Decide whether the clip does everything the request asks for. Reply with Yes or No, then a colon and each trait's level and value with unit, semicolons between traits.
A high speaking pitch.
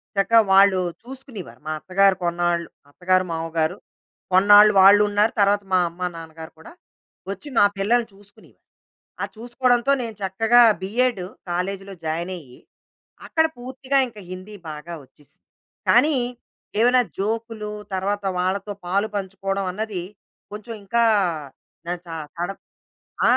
Yes: high, 200 Hz